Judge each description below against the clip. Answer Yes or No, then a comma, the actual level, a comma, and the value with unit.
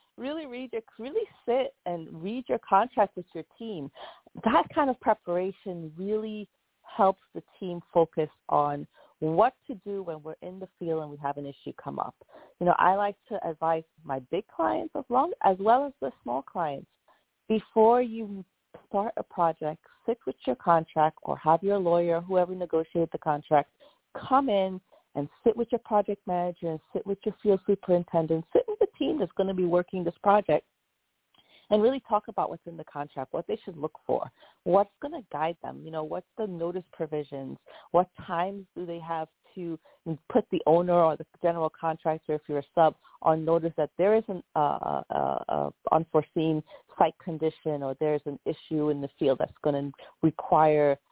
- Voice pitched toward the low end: No, medium, 175 Hz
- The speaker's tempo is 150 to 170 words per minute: No, average, 190 wpm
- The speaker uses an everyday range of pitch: Yes, average, 4.8 semitones